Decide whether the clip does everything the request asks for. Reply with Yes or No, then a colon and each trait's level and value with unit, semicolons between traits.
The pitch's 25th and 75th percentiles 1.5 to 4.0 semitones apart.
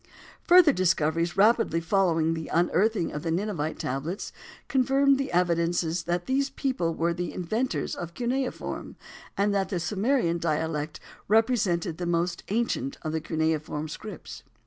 No: average, 5.2 semitones